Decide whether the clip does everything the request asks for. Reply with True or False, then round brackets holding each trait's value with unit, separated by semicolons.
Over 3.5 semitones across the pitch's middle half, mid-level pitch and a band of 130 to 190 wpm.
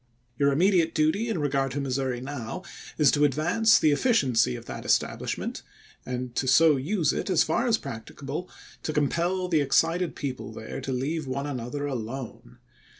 True (4.1 semitones; 145 Hz; 170 wpm)